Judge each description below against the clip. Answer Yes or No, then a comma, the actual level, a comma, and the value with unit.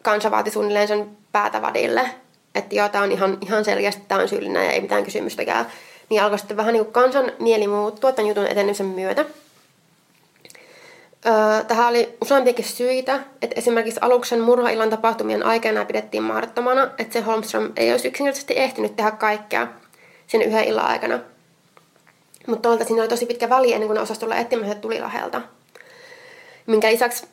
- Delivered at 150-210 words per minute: Yes, fast, 155 wpm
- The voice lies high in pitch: Yes, high, 225 Hz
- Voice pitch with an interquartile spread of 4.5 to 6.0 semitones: No, average, 3.2 semitones